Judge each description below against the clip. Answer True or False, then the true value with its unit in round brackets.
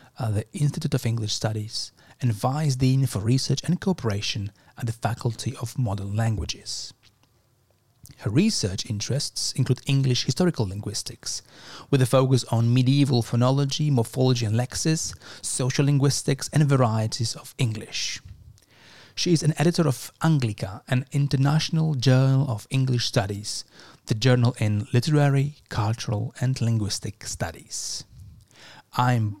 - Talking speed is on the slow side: True (125 wpm)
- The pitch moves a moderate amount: True (3.6 semitones)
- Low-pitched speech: True (125 Hz)